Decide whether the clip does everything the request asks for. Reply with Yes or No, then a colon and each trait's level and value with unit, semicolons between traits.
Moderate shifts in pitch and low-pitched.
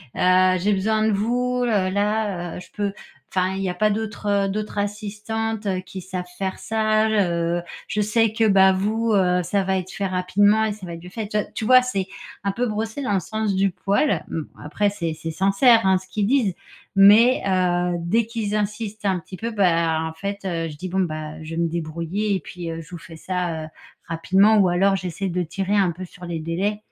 No: average, 3.1 semitones; high, 195 Hz